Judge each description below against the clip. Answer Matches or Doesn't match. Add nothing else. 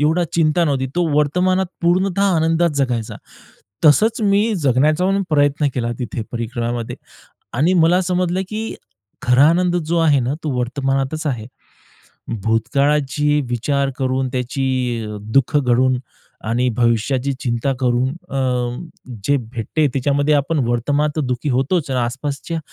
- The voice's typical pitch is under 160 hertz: Matches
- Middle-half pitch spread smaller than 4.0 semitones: Doesn't match